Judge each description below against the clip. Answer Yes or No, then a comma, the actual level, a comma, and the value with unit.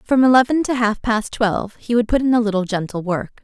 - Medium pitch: No, high, 225 Hz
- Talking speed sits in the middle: No, fast, 245 wpm